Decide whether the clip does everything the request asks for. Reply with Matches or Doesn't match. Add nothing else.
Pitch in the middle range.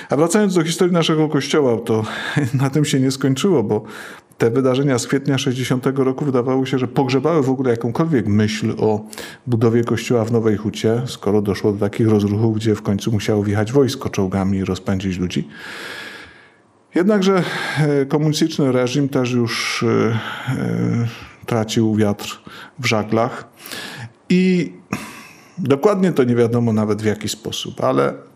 Doesn't match